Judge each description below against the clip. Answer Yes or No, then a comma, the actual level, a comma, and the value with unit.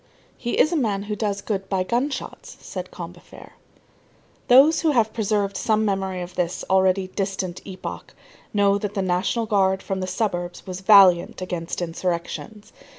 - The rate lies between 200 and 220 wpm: No, average, 160 wpm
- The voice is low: No, high, 195 Hz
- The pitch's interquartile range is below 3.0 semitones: Yes, narrow, 2.6 semitones